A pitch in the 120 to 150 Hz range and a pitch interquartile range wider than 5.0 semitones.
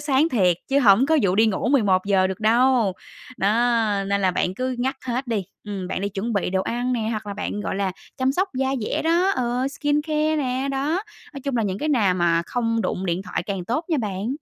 No: high, 230 Hz; wide, 5.5 semitones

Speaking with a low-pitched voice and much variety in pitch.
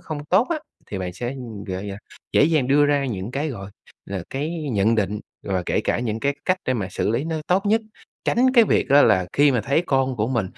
Yes: low, 130 Hz; wide, 6.3 semitones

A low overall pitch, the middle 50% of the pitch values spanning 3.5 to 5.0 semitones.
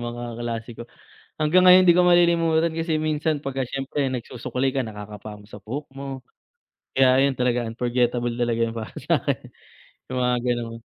Yes: low, 125 Hz; average, 4.5 semitones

